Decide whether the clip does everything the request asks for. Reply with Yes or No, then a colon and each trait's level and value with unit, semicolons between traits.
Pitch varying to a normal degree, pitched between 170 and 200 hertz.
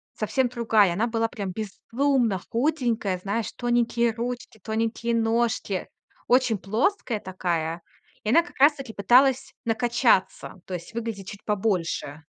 No: average, 3.4 semitones; high, 225 Hz